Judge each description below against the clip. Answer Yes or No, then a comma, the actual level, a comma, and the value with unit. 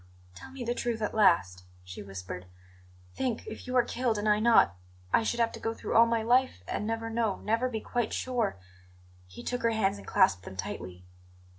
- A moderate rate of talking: No, fast, 210 wpm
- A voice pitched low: No, high, 220 Hz